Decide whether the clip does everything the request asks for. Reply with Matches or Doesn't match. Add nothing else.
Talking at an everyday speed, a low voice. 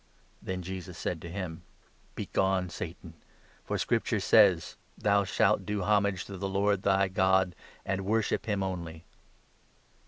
Matches